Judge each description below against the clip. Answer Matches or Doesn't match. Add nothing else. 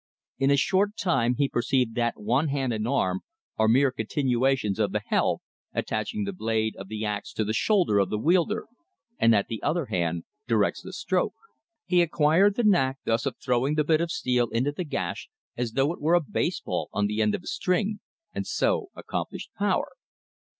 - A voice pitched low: Matches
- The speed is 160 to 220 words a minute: Matches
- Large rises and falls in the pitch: Matches